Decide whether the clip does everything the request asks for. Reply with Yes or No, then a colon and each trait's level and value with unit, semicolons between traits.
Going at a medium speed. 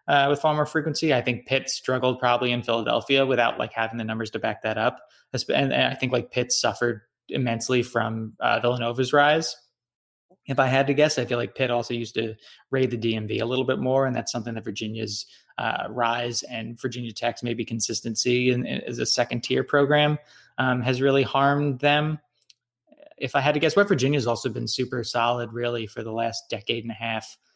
No: fast, 210 wpm